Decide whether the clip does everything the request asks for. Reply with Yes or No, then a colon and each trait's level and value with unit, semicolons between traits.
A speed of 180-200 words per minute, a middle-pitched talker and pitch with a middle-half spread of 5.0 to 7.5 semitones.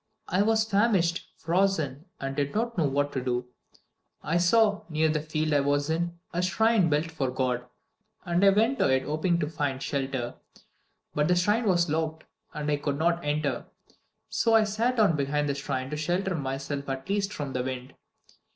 Yes: average, 190 wpm; medium, 155 Hz; average, 5.3 semitones